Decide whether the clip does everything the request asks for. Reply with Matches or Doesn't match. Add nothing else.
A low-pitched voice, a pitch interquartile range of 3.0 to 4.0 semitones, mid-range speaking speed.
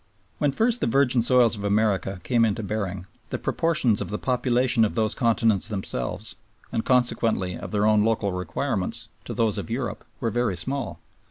Matches